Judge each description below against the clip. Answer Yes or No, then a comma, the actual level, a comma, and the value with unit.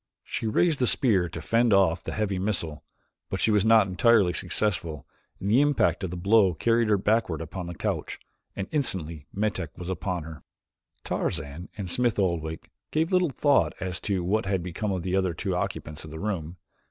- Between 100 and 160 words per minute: No, average, 190 wpm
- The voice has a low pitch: Yes, very low, 95 Hz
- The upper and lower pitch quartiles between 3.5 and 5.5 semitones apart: Yes, average, 4.4 semitones